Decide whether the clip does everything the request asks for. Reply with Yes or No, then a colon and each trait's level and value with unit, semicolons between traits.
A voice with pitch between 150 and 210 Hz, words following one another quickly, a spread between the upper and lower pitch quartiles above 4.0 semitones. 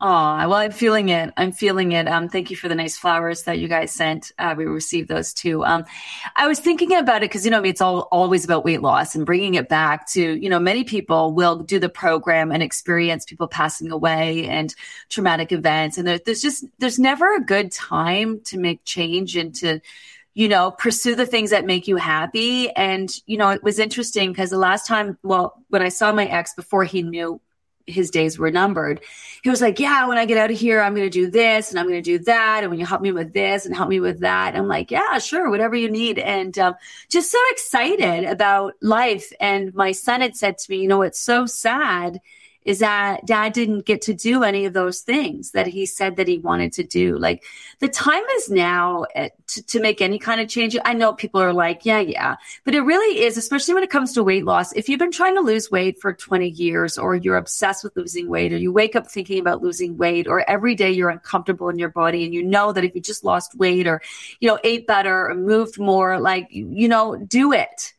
Yes: high, 190 Hz; fast, 240 wpm; average, 4.4 semitones